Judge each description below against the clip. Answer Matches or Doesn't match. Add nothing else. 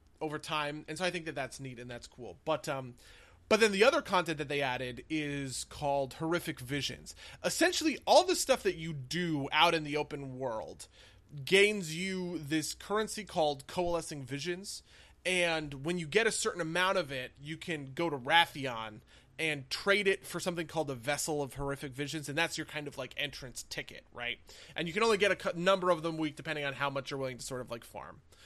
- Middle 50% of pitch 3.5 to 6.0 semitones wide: Matches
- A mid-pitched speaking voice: Matches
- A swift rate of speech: Matches